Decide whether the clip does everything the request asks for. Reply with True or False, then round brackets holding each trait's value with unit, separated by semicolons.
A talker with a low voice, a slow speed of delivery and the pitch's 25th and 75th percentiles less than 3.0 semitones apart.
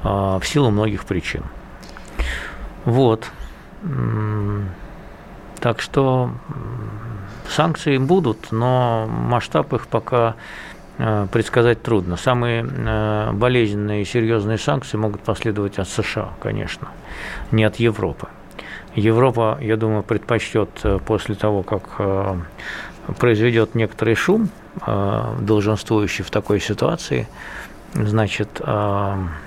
True (110 Hz; 90 wpm; 2.4 semitones)